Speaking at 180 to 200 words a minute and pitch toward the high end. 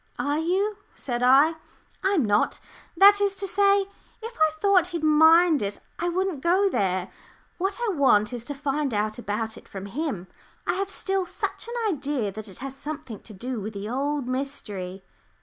Yes: average, 185 wpm; very high, 290 Hz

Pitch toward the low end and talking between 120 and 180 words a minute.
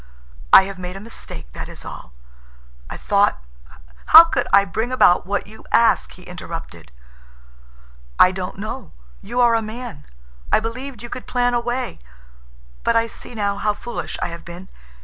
No: high, 215 Hz; average, 170 wpm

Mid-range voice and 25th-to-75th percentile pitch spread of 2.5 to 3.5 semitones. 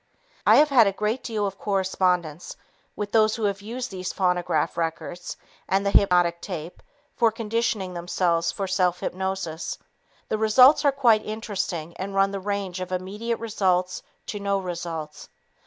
No: high, 195 Hz; average, 3.2 semitones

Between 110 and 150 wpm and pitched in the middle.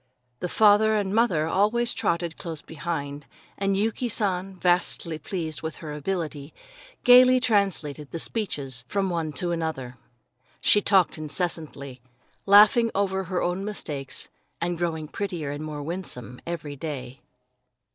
Yes: slow, 135 wpm; medium, 170 Hz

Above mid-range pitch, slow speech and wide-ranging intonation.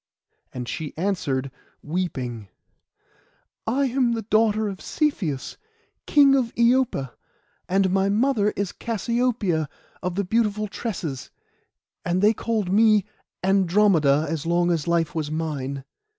Yes: high, 195 Hz; slow, 120 wpm; wide, 6.0 semitones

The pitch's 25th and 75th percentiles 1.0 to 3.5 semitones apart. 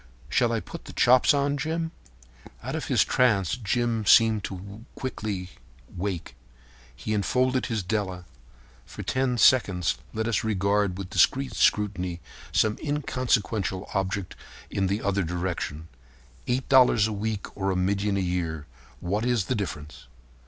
No: average, 4.6 semitones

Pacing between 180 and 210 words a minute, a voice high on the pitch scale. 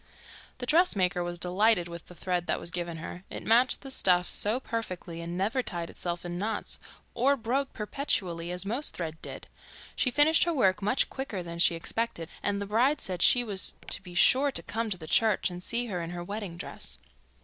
Yes: fast, 205 wpm; high, 195 Hz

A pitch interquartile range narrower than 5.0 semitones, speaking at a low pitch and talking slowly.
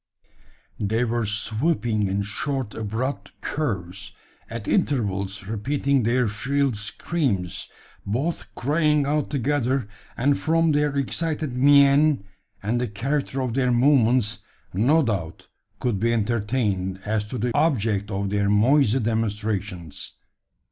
No: average, 5.3 semitones; low, 120 Hz; slow, 120 wpm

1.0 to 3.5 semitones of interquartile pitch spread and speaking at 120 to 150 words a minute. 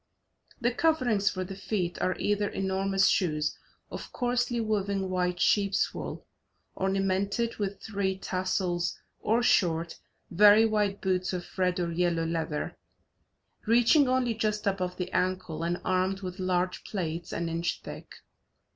Yes: average, 2.7 semitones; average, 140 wpm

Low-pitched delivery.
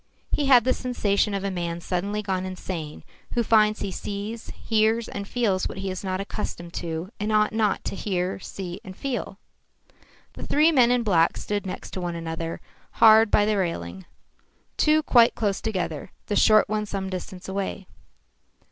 No: high, 200 Hz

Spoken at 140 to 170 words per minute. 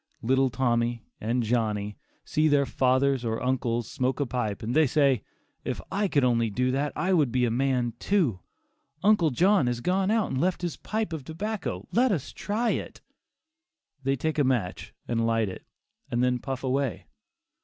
No: average, 180 wpm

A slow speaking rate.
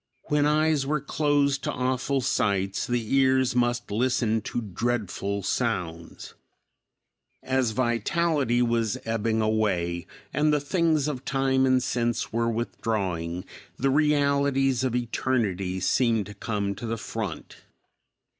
Yes: slow, 125 wpm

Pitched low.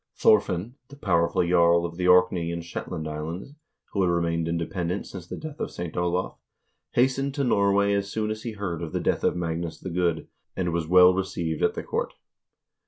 Yes: very low, 90 Hz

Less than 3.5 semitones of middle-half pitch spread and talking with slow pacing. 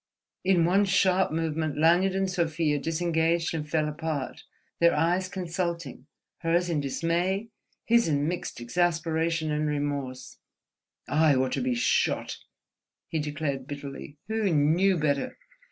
Yes: average, 3.1 semitones; slow, 125 wpm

